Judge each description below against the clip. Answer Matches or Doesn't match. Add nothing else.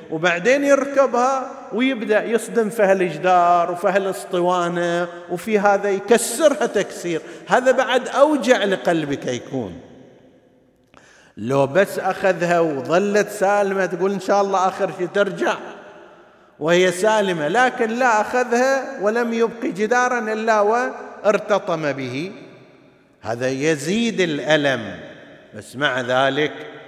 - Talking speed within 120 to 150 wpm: Doesn't match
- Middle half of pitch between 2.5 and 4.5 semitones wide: Doesn't match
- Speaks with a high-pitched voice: Matches